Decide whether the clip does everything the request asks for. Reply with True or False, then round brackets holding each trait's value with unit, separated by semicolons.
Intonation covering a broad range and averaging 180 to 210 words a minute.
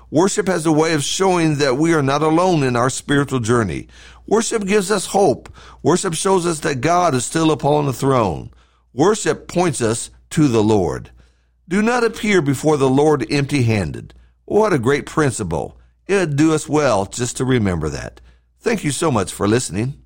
True (6.8 semitones; 185 wpm)